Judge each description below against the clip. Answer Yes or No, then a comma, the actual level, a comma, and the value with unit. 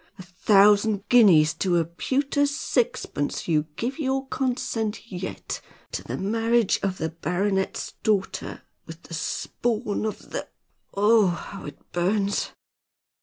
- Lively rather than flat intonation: No, average, 4.5 semitones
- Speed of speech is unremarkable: No, slow, 125 wpm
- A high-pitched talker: Yes, high, 200 Hz